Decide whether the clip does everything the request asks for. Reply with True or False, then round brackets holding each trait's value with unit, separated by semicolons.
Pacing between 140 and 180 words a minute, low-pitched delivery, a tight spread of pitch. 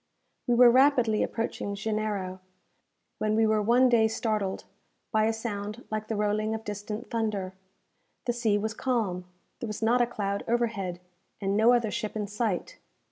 False (165 wpm; 215 Hz; 2.1 semitones)